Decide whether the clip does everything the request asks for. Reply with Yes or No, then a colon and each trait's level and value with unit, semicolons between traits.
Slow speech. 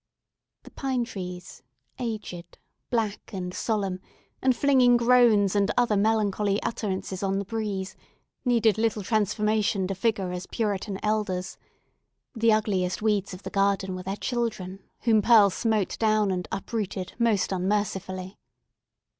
Yes: slow, 130 wpm